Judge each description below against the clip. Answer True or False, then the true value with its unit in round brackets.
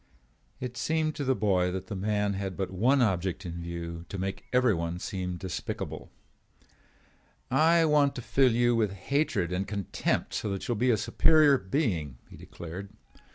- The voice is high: False (100 Hz)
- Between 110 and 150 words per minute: False (170 wpm)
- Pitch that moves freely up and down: True (5.7 semitones)